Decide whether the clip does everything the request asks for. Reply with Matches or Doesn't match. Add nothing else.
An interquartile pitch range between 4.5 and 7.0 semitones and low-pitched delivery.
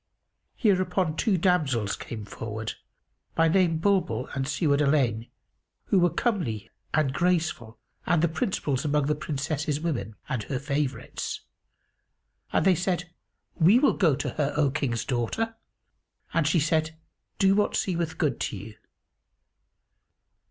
Doesn't match